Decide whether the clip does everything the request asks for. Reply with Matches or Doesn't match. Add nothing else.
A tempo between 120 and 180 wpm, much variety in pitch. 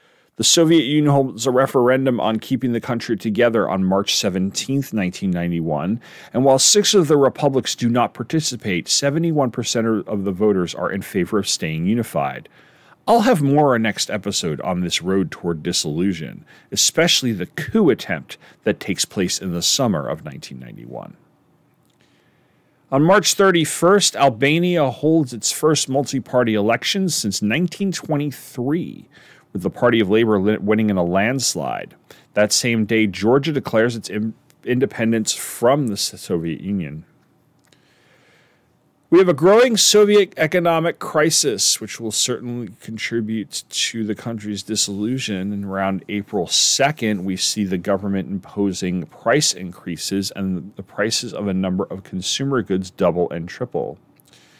Matches